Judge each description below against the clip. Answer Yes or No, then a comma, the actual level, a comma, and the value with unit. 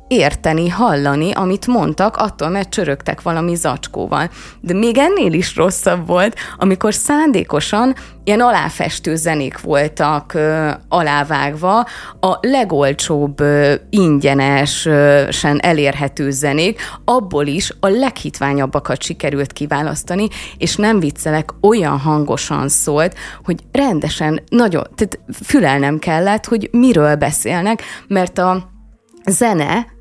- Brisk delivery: No, slow, 105 wpm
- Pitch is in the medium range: Yes, medium, 165 Hz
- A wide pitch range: Yes, wide, 6.5 semitones